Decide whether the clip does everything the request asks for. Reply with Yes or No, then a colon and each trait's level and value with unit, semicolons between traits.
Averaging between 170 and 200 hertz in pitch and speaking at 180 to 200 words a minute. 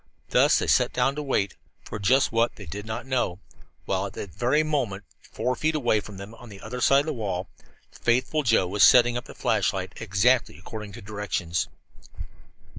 No: low, 115 Hz; average, 190 wpm